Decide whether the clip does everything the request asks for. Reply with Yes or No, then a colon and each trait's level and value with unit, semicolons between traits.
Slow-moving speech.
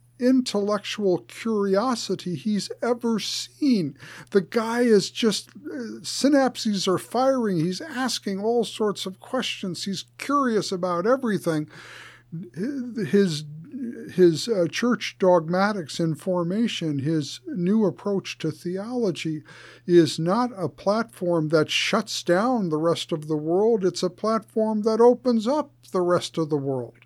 Yes: slow, 125 wpm